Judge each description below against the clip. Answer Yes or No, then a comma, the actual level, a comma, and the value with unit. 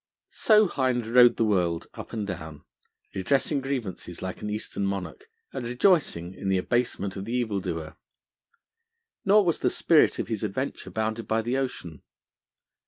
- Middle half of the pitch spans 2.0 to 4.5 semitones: No, wide, 5.4 semitones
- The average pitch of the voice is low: Yes, low, 110 Hz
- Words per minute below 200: Yes, average, 155 wpm